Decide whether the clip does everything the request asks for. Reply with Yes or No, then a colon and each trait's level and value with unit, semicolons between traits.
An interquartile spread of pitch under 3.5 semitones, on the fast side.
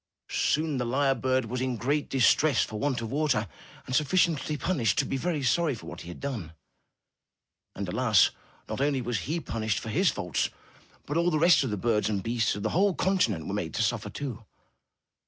No: wide, 5.5 semitones; fast, 210 wpm